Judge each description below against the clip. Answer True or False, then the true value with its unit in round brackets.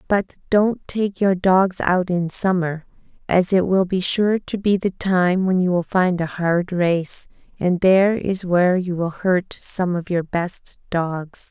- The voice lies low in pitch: False (180 Hz)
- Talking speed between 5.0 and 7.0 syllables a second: False (3.8 syllables/s)